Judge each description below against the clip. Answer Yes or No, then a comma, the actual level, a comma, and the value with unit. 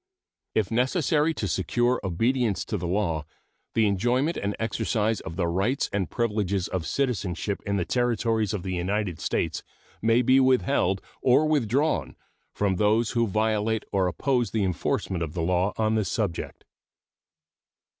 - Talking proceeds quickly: No, average, 150 wpm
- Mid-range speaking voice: No, low, 105 Hz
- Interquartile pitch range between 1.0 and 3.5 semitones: No, average, 4.5 semitones